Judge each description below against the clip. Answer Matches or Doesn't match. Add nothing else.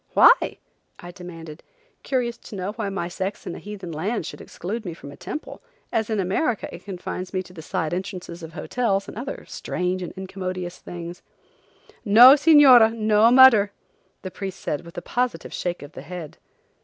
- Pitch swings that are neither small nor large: Matches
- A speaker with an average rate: Matches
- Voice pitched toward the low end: Doesn't match